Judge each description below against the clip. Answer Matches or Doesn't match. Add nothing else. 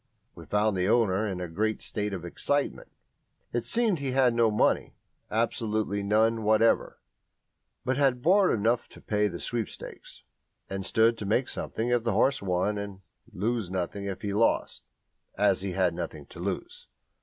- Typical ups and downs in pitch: Matches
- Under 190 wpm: Matches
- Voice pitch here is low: Matches